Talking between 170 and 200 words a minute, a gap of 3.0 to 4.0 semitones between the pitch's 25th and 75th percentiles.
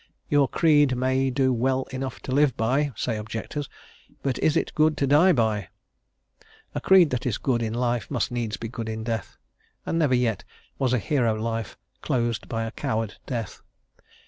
Yes: average, 180 wpm; average, 3.5 semitones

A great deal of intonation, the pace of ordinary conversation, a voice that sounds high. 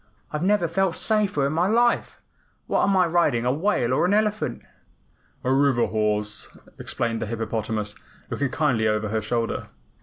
No: wide, 8.4 semitones; average, 160 wpm; low, 135 Hz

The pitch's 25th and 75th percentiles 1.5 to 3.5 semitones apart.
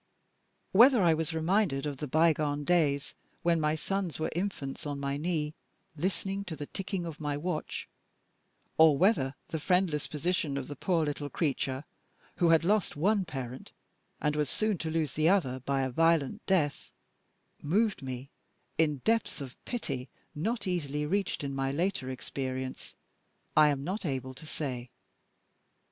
No: average, 4.3 semitones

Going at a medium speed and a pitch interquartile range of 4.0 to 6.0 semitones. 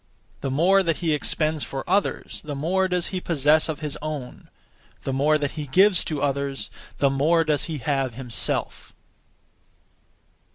No: average, 160 wpm; average, 3.2 semitones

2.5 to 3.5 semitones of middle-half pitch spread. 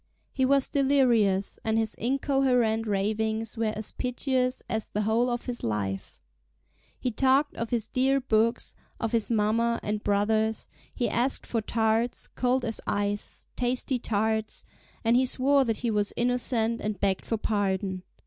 Yes: average, 2.8 semitones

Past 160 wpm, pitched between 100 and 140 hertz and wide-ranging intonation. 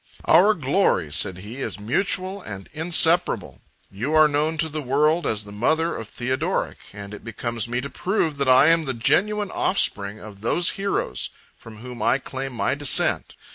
Yes: average, 175 wpm; low, 135 Hz; wide, 6.5 semitones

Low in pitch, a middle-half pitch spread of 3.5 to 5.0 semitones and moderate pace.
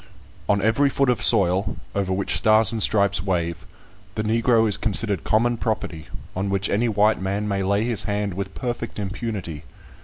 No: low, 105 Hz; narrow, 2.6 semitones; average, 175 wpm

